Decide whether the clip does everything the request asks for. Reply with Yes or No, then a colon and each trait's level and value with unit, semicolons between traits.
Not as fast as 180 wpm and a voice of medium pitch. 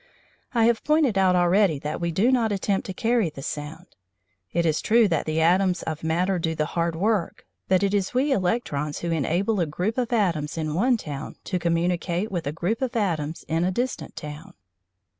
No: average, 200 wpm; medium, 180 Hz